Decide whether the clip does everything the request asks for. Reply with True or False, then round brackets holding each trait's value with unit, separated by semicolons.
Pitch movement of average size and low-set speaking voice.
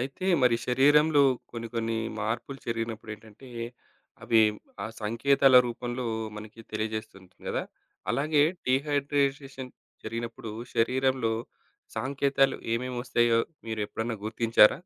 True (3.2 semitones; 120 Hz)